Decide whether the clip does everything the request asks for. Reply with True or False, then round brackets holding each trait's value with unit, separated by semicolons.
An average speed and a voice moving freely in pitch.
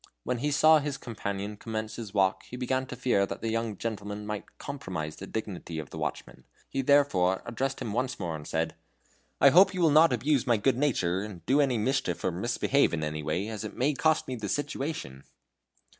False (210 wpm; 5.9 semitones)